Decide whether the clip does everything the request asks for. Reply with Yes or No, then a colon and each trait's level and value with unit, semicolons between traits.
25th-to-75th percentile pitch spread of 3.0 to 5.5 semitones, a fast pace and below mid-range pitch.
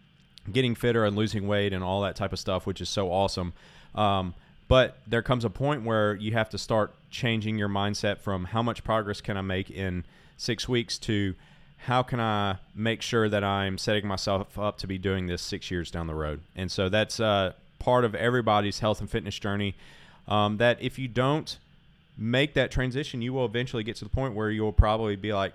Yes: average, 3.3 semitones; fast, 215 wpm; low, 105 Hz